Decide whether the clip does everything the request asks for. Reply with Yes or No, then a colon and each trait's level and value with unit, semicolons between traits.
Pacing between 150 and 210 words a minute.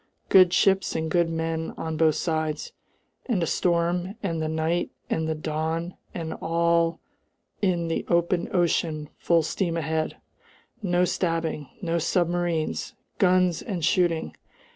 No: slow, 135 wpm